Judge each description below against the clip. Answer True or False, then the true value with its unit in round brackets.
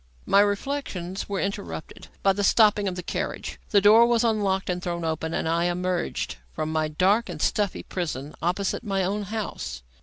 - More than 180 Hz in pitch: True (190 Hz)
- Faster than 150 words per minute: True (180 wpm)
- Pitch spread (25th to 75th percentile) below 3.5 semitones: True (3.1 semitones)